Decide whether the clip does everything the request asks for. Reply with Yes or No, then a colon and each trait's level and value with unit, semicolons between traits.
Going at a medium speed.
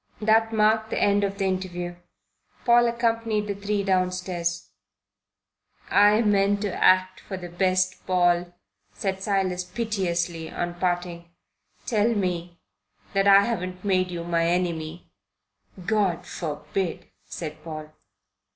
No: slow, 125 wpm